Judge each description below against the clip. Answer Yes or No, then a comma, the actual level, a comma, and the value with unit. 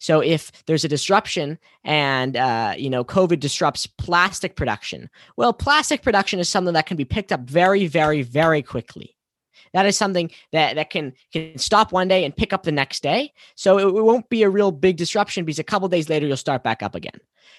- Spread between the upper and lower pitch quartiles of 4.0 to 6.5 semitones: Yes, average, 4.6 semitones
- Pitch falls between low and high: Yes, medium, 175 Hz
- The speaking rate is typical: No, fast, 215 wpm